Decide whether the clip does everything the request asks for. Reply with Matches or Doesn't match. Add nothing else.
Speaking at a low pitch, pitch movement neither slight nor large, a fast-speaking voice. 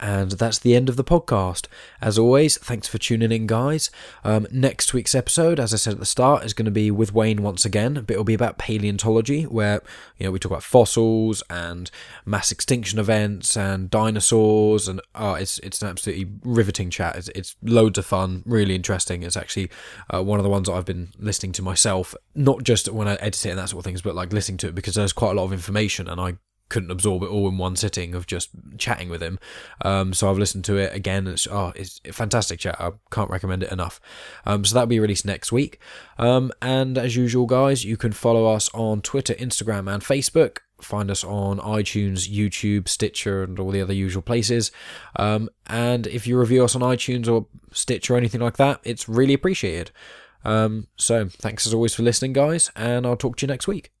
Matches